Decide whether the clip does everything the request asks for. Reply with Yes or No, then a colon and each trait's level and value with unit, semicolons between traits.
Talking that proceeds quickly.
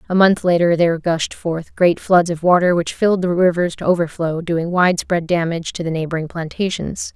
No: average, 195 wpm